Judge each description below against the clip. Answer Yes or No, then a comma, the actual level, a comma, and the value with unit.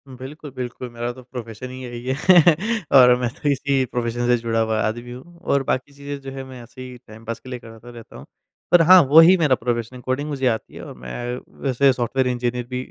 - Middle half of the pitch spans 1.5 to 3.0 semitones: Yes, narrow, 2.6 semitones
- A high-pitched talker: No, low, 125 Hz